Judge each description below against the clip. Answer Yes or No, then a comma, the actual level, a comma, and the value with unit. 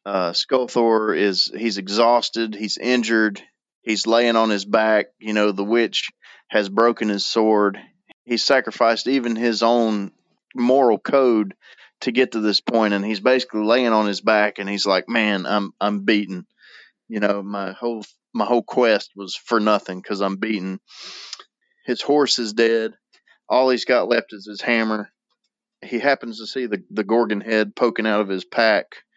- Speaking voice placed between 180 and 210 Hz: No, low, 110 Hz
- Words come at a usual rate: Yes, average, 165 wpm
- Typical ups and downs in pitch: No, narrow, 2.3 semitones